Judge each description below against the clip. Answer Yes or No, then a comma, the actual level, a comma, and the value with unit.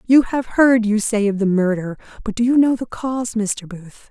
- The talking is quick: Yes, fast, 235 wpm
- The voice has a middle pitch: No, high, 220 Hz